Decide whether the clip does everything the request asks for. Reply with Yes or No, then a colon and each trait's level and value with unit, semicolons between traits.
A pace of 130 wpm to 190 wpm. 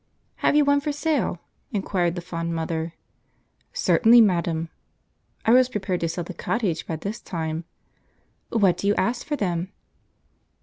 Yes: average, 150 wpm